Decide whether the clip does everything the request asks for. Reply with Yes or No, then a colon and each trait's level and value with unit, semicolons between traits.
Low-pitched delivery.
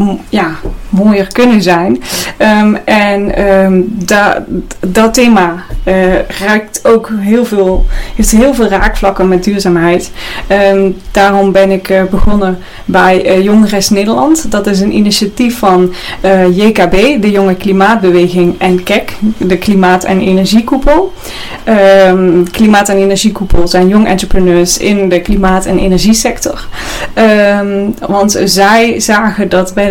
No: high, 195 Hz